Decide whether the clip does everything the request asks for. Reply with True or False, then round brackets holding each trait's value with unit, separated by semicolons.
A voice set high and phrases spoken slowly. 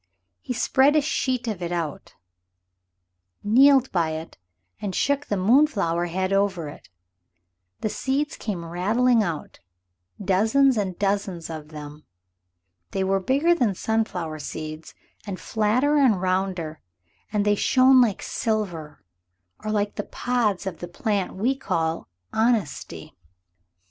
True (205 Hz; 130 wpm)